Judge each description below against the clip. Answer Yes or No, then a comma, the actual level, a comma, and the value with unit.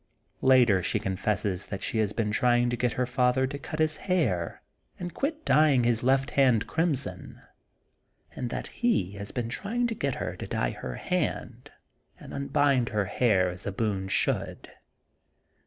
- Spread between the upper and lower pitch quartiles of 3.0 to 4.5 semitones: No, wide, 5.4 semitones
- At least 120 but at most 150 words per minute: No, average, 170 wpm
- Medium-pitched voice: No, low, 120 Hz